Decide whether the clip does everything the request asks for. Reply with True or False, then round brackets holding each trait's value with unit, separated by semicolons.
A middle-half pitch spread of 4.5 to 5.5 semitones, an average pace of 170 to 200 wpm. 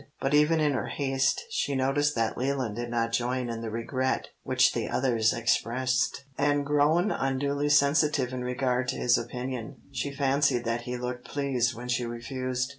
False (2.7 semitones; 175 wpm)